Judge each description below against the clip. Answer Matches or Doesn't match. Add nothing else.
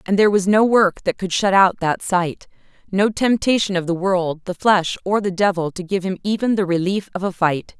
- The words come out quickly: Matches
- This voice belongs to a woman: Matches